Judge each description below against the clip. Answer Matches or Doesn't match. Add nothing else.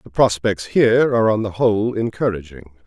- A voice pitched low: Matches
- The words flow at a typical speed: Matches